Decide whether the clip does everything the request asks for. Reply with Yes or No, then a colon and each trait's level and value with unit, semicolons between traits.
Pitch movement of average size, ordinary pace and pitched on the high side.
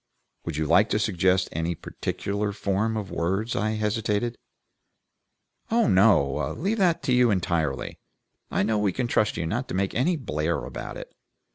No: average, 4.6 semitones; average, 165 wpm; low, 105 Hz